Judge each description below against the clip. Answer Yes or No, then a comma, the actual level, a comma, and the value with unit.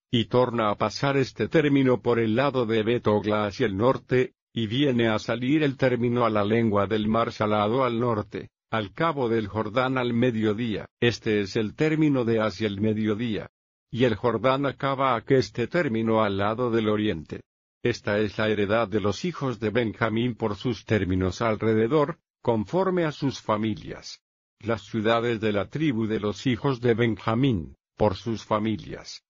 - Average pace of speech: Yes, average, 170 wpm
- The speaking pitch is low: Yes, low, 115 Hz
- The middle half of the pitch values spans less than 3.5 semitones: Yes, average, 2.9 semitones